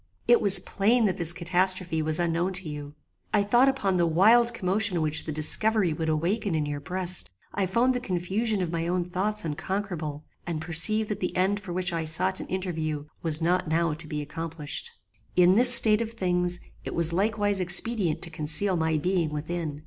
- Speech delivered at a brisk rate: No, average, 195 wpm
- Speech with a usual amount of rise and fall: Yes, average, 3.9 semitones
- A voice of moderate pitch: Yes, medium, 180 Hz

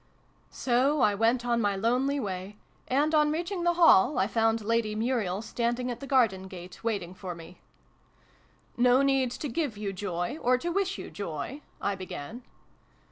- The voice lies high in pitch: Yes, high, 235 Hz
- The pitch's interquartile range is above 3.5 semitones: Yes, wide, 5.4 semitones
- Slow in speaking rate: No, average, 185 wpm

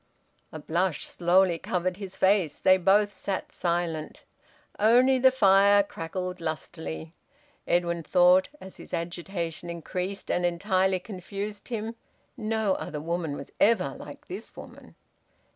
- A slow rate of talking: Yes, slow, 125 wpm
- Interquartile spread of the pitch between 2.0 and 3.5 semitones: Yes, average, 2.8 semitones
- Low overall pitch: No, medium, 185 Hz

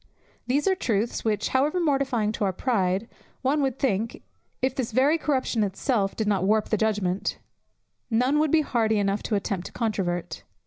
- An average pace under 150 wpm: No, average, 175 wpm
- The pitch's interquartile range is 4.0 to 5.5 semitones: Yes, average, 4.8 semitones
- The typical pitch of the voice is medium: No, high, 225 Hz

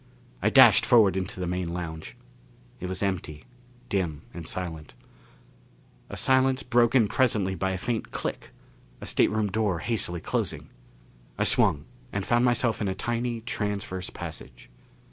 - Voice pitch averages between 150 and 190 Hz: No, low, 100 Hz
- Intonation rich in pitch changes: No, average, 4.8 semitones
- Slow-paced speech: No, average, 145 wpm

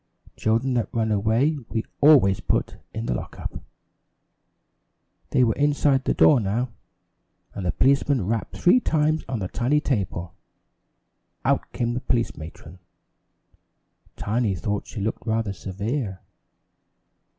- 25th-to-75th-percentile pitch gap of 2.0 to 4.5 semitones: No, average, 5.0 semitones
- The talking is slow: Yes, slow, 130 wpm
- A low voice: Yes, low, 115 Hz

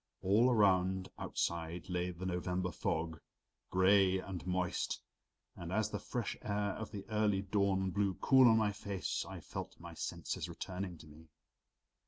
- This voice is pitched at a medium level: No, very low, 95 Hz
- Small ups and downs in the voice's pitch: Yes, narrow, 2.3 semitones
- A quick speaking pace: No, average, 155 wpm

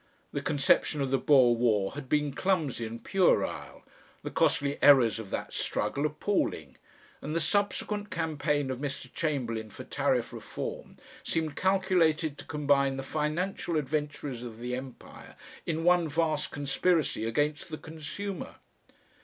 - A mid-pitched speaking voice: Yes, medium, 150 Hz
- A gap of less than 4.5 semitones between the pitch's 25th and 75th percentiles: Yes, average, 3.7 semitones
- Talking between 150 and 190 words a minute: No, average, 140 wpm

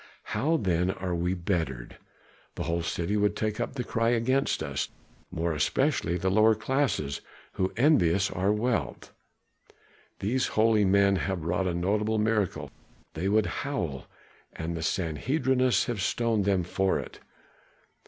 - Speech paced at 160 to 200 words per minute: No, average, 145 wpm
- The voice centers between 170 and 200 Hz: No, low, 100 Hz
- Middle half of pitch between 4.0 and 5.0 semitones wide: Yes, average, 4.7 semitones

